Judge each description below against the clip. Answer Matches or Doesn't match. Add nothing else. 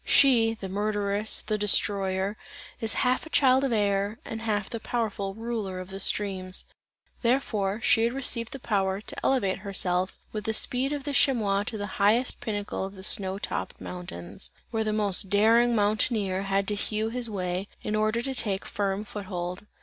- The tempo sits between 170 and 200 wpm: Matches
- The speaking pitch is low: Doesn't match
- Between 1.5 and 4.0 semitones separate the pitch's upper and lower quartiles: Matches